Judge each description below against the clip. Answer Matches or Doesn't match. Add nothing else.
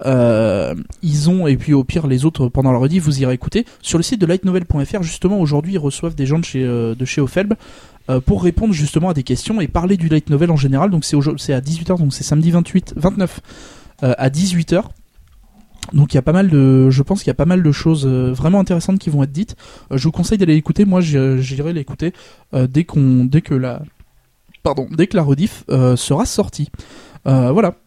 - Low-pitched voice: Doesn't match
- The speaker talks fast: Matches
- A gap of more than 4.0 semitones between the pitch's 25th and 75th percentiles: Matches